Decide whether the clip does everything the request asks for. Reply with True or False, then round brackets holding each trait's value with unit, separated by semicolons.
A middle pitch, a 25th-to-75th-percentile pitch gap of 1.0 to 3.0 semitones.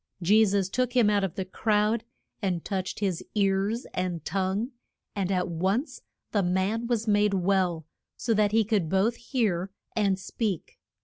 False (200 Hz; 2.6 semitones)